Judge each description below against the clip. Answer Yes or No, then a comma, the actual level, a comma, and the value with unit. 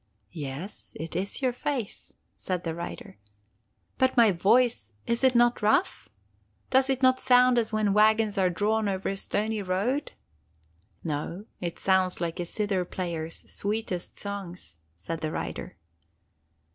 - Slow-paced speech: No, average, 145 wpm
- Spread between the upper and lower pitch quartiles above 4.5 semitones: Yes, average, 5.1 semitones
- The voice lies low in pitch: No, high, 200 Hz